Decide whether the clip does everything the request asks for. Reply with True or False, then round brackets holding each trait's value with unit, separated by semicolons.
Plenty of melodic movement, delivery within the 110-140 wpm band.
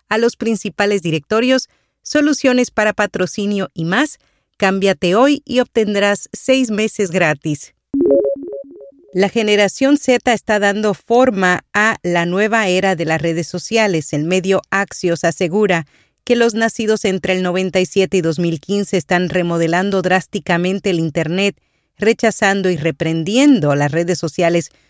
False (4.2 semitones; 130 wpm)